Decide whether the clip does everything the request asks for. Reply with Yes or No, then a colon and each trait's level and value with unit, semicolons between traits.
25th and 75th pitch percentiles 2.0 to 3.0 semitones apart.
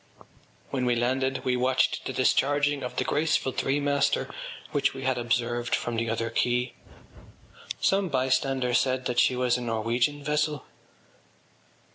Yes: narrow, 2.4 semitones